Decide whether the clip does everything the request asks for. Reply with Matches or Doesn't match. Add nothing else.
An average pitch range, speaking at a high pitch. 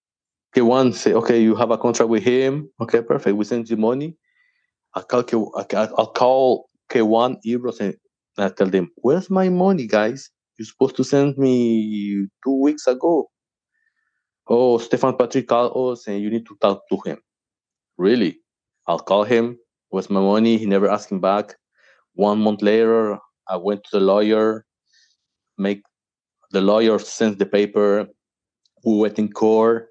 Doesn't match